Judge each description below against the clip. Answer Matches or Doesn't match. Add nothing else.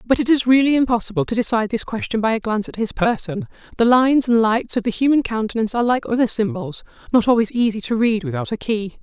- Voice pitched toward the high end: Matches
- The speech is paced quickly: Matches